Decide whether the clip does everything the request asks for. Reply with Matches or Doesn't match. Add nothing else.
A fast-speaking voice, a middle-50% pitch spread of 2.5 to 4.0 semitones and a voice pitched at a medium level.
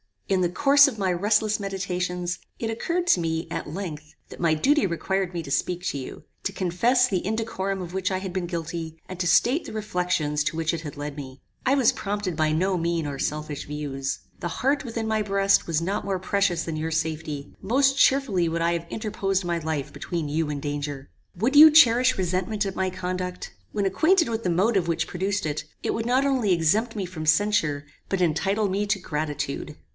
Doesn't match